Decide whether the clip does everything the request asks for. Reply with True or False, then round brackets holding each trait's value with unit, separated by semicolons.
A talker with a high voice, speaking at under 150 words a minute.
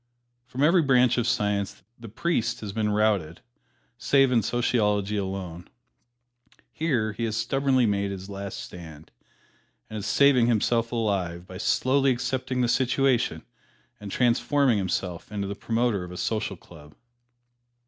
False (110 Hz; 140 wpm)